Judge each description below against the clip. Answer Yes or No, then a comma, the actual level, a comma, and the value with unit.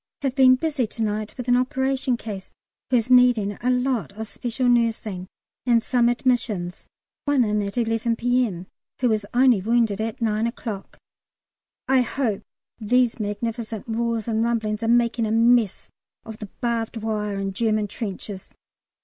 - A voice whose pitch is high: Yes, high, 230 Hz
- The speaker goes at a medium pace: Yes, average, 160 wpm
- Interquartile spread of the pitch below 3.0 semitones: Yes, narrow, 2.5 semitones